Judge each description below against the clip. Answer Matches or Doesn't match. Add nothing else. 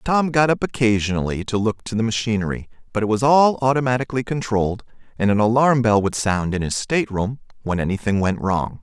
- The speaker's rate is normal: Matches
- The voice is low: Matches